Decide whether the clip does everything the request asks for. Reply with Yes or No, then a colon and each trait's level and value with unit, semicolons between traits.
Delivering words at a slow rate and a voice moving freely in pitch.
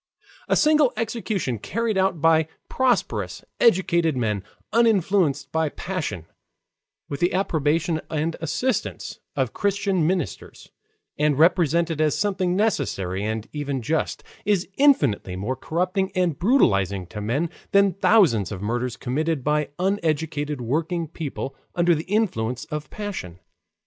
Yes: slow, 125 wpm; wide, 6.4 semitones